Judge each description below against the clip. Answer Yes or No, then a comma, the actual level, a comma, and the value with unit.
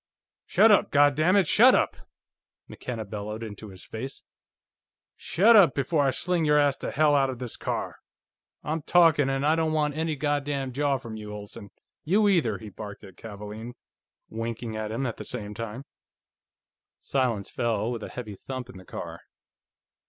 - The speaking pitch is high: No, low, 130 Hz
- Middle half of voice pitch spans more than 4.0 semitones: Yes, average, 5.3 semitones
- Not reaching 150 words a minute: No, average, 170 wpm